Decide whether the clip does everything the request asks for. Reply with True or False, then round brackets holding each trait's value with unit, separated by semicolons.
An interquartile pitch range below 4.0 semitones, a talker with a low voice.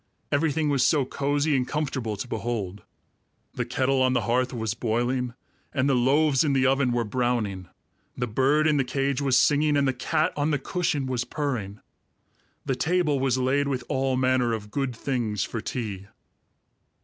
True (2.9 semitones; 130 Hz)